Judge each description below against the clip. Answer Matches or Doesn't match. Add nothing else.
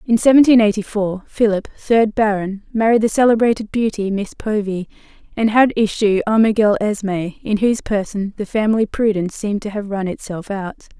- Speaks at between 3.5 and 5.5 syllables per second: Matches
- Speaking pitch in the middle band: Doesn't match